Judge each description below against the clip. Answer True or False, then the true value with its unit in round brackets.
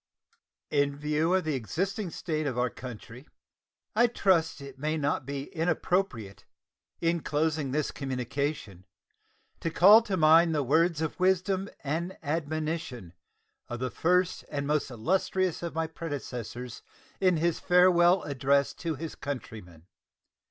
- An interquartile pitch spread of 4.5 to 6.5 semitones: False (4.1 semitones)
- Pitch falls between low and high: True (155 Hz)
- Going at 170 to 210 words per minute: False (135 wpm)